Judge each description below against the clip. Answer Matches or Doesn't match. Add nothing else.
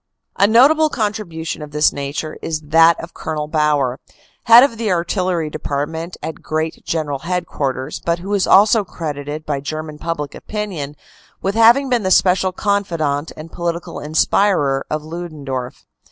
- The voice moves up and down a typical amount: Matches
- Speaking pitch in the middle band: Matches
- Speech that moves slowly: Doesn't match